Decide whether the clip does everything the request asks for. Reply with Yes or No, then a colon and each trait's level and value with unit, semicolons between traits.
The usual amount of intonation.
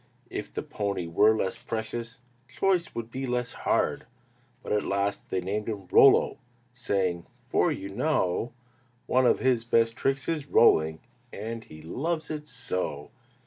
Yes: average, 4.8 semitones